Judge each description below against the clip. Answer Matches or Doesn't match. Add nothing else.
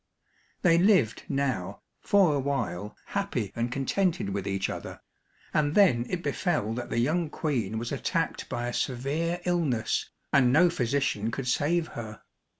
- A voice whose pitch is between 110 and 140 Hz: Matches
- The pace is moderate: Matches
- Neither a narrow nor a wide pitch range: Doesn't match